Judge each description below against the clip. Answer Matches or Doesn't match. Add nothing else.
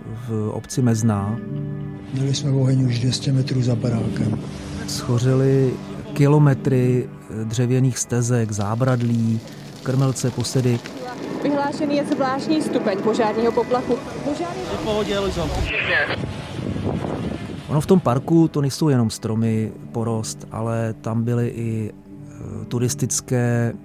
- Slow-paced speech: Matches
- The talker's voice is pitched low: Matches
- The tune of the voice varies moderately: Matches